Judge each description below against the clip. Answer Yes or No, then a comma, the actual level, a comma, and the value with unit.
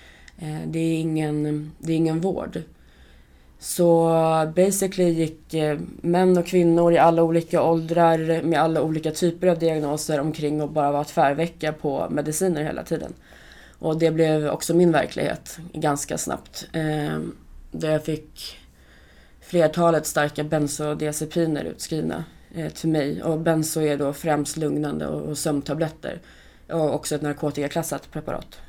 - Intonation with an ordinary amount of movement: No, narrow, 2.0 semitones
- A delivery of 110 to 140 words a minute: Yes, average, 130 wpm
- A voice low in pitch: No, medium, 155 Hz